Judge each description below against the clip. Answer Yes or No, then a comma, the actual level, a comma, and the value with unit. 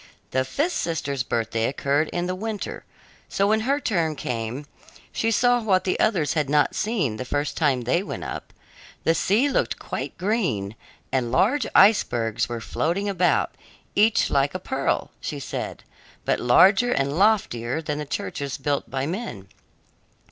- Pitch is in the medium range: Yes, medium, 160 Hz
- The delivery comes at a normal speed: Yes, average, 160 wpm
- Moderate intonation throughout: No, wide, 7.7 semitones